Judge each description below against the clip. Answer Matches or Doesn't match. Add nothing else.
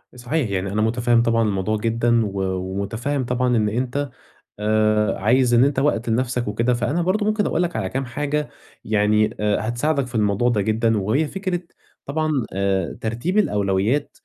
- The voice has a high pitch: Doesn't match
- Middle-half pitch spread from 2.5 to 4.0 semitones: Doesn't match